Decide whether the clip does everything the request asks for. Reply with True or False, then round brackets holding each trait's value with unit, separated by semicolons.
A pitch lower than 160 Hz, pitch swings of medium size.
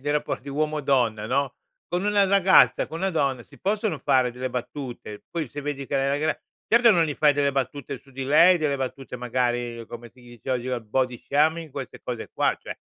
True (140 Hz; 3.7 semitones)